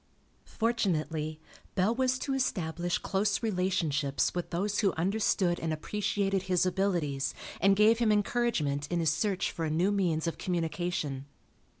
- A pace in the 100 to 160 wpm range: Yes, average, 140 wpm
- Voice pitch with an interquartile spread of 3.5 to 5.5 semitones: Yes, average, 4.4 semitones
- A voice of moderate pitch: Yes, medium, 180 Hz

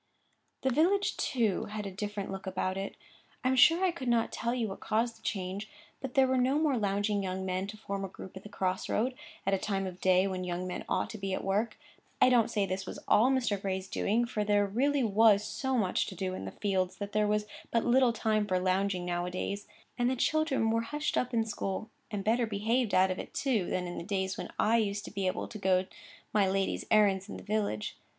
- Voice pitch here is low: No, high, 205 Hz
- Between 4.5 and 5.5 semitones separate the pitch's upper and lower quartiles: No, average, 3.5 semitones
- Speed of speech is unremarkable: No, fast, 245 wpm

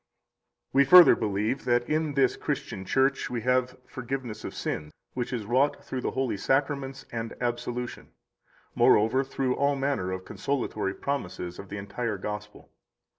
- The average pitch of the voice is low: Yes, low, 125 Hz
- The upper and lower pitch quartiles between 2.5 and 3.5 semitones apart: No, average, 4.3 semitones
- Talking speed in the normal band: Yes, average, 155 wpm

